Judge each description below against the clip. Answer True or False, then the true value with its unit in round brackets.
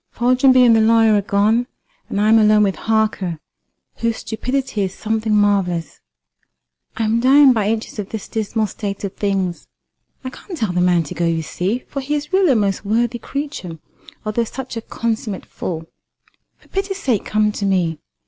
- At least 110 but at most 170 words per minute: False (185 wpm)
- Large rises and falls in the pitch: False (3.3 semitones)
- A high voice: True (220 Hz)